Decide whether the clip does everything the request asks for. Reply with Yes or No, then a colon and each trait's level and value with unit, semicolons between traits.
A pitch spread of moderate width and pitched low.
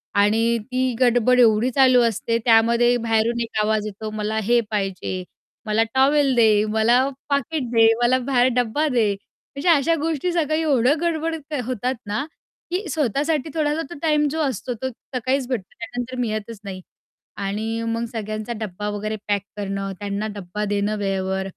No: average, 3.9 semitones; high, 235 Hz